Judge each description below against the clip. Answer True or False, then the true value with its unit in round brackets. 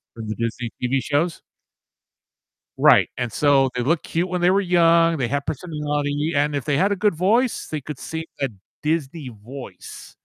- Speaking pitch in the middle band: True (150 Hz)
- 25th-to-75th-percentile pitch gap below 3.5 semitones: False (3.8 semitones)